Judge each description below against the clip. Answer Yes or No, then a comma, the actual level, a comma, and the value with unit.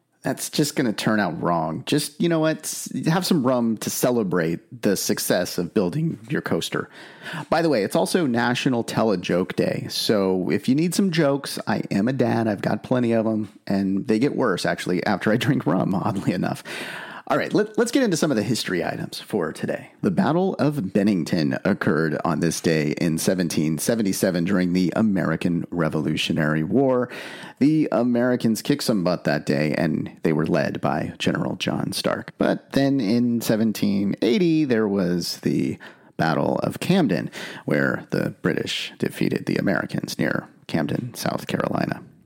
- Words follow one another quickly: No, average, 170 wpm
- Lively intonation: Yes, wide, 7.6 semitones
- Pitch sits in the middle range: No, low, 110 Hz